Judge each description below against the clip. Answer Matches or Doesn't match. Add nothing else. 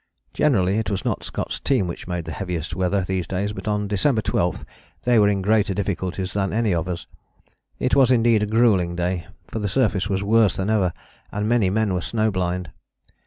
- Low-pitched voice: Matches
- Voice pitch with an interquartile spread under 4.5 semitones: Matches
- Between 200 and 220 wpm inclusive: Matches